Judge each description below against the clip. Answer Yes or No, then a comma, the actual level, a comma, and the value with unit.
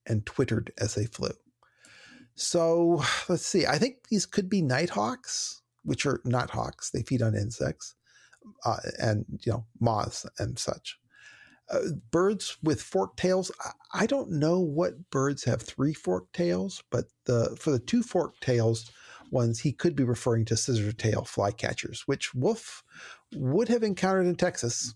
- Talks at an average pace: Yes, average, 160 wpm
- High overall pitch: No, medium, 140 Hz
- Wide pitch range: Yes, wide, 7.5 semitones